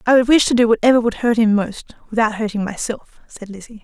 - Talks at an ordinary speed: No, fast, 220 wpm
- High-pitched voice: Yes, high, 220 Hz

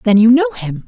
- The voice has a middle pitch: No, high, 235 Hz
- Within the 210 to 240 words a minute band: No, fast, 275 wpm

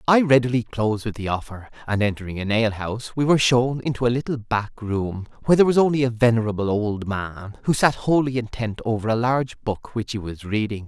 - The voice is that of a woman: No, male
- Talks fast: Yes, fast, 215 wpm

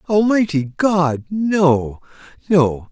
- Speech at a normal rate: No, slow, 60 wpm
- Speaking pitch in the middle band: Yes, medium, 165 Hz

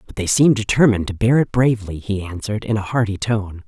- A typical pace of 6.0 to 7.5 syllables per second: Yes, 6.2 syllables/s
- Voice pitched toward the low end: Yes, low, 105 Hz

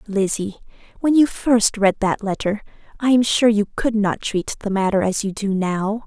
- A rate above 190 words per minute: Yes, average, 200 wpm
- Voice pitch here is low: No, high, 210 Hz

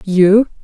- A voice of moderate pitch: No, high, 200 Hz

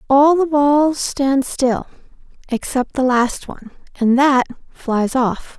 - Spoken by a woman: Yes, female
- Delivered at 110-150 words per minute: Yes, average, 140 wpm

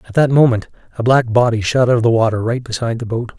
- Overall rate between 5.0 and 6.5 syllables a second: No, 7.0 syllables/s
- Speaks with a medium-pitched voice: No, low, 120 Hz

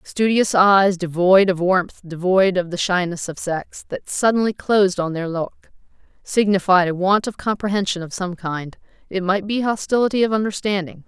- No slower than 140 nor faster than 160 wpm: No, average, 170 wpm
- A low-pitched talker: No, high, 190 Hz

